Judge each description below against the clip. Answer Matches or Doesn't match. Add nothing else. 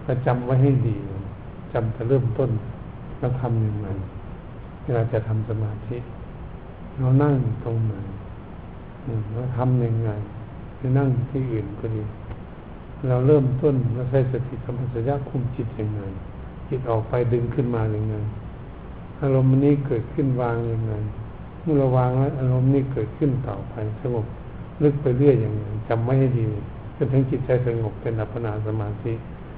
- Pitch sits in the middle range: Doesn't match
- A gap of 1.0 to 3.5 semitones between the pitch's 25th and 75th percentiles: Matches